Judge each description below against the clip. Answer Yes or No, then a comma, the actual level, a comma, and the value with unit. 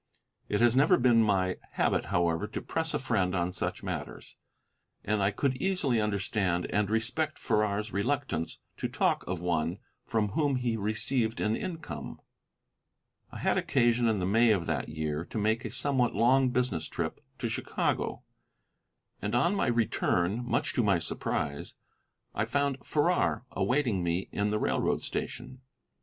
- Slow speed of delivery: No, average, 155 wpm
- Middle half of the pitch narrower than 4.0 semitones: No, average, 5.0 semitones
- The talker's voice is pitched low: Yes, low, 110 Hz